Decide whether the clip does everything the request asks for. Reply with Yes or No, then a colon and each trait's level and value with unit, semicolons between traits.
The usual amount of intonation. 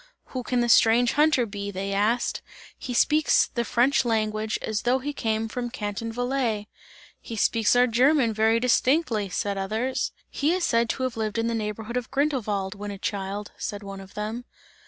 Yes: average, 3.1 semitones